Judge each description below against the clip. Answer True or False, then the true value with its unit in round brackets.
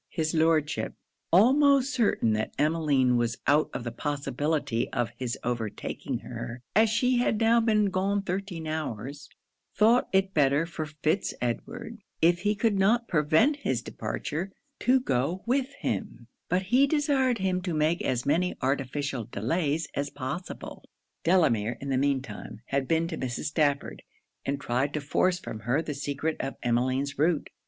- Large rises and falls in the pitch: True (6.3 semitones)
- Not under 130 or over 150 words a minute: False (160 wpm)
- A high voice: False (155 Hz)